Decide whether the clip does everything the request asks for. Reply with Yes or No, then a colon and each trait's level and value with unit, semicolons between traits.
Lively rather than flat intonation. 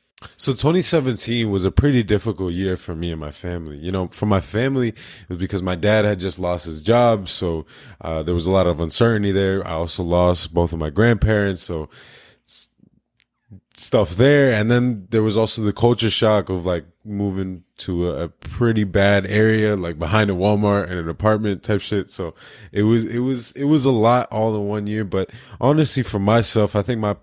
No: average, 3.6 semitones